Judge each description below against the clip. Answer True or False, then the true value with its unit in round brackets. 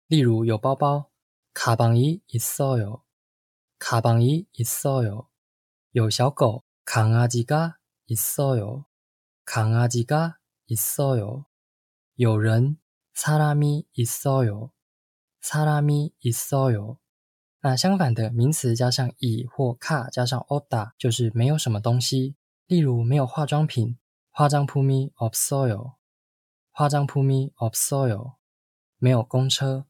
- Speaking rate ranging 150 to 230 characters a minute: True (195 characters per minute)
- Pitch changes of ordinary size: True (3.7 semitones)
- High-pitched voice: False (125 Hz)